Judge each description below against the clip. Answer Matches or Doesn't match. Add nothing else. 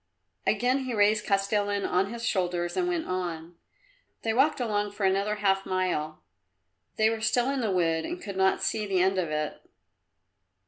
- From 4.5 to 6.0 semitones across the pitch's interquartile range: Doesn't match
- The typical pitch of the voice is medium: Doesn't match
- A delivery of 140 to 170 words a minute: Doesn't match